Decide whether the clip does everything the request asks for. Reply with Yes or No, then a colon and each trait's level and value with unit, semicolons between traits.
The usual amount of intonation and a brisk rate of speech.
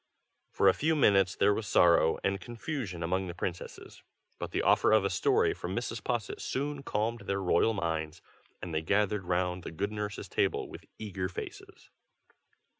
No: average, 3.9 semitones; average, 175 wpm